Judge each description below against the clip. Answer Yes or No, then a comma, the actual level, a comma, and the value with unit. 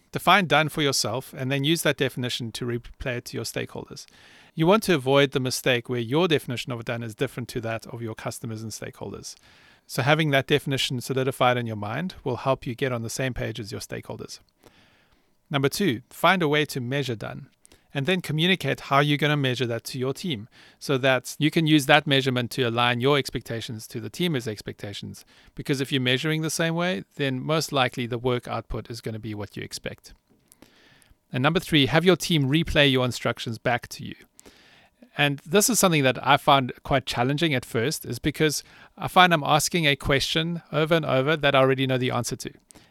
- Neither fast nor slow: No, fast, 210 wpm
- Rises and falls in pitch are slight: No, average, 3.7 semitones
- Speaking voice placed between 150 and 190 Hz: No, low, 135 Hz